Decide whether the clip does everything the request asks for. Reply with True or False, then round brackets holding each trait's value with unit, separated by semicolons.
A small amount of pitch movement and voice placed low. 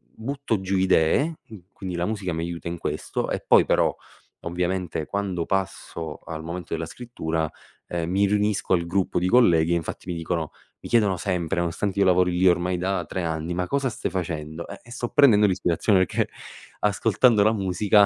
False (3.2 semitones; 90 Hz)